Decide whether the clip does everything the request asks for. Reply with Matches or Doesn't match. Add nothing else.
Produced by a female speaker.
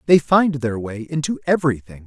Doesn't match